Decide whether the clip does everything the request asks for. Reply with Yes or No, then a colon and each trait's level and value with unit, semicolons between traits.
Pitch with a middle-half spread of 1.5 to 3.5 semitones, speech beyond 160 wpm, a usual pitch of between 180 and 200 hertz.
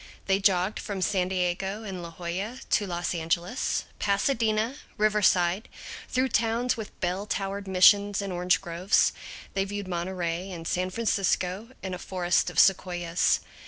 No: narrow, 2.5 semitones; average, 145 wpm; high, 190 Hz